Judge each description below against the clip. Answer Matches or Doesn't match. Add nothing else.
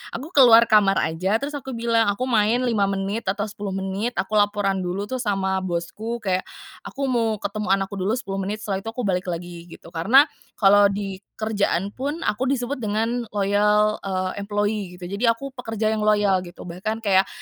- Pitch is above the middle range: Matches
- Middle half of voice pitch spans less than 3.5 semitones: Matches